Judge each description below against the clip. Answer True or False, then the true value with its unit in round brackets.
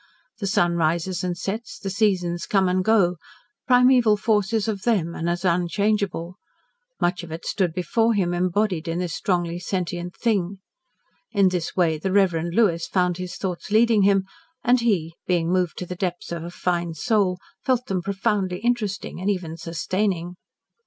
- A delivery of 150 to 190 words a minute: True (170 wpm)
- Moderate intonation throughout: True (3.0 semitones)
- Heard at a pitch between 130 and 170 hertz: False (185 Hz)